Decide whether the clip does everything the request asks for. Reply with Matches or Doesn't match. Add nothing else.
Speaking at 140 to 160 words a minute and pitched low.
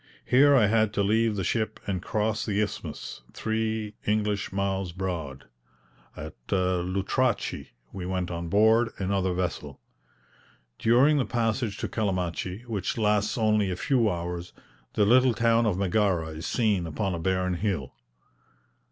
Matches